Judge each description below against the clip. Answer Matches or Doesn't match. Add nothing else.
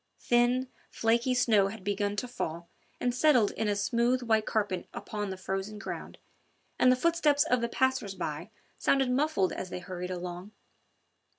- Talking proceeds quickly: Doesn't match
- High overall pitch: Matches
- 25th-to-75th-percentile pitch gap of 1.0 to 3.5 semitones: Doesn't match